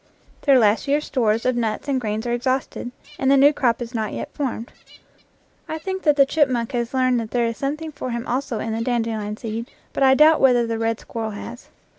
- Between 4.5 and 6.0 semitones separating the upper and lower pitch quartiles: No, average, 3.1 semitones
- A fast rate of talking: Yes, fast, 220 wpm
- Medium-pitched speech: No, high, 245 Hz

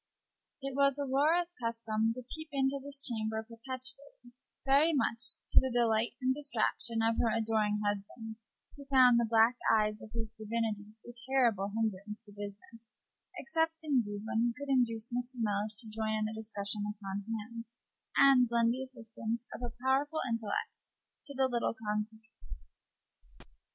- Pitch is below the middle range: No, high, 230 Hz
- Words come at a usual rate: Yes, average, 155 wpm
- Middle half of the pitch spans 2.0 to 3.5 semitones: Yes, average, 3.2 semitones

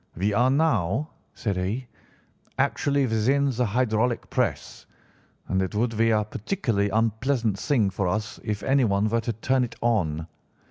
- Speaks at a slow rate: No, average, 150 wpm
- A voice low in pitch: Yes, low, 115 Hz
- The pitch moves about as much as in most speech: Yes, average, 3.7 semitones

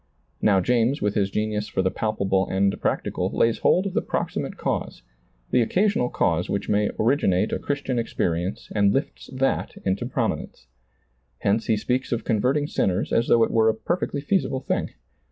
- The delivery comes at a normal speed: Yes, average, 170 wpm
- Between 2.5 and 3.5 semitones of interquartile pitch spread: No, average, 4.6 semitones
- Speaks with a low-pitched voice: Yes, low, 110 Hz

